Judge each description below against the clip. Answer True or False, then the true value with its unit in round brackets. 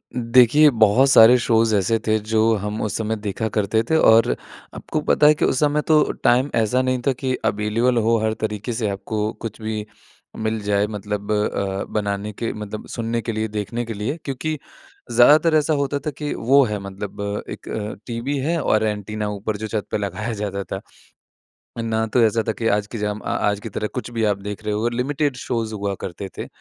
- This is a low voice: True (110 Hz)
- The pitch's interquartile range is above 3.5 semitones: False (2.8 semitones)